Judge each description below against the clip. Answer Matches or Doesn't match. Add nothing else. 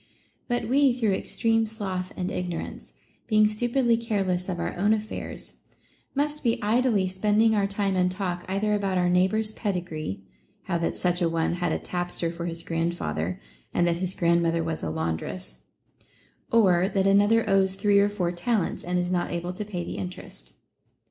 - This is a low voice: Doesn't match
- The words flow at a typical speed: Matches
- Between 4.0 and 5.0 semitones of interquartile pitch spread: Doesn't match